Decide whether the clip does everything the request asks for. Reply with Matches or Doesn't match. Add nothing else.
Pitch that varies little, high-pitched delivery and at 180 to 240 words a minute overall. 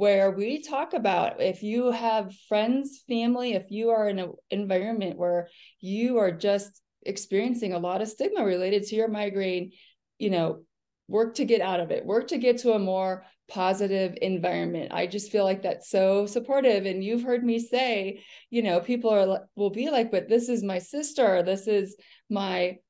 Doesn't match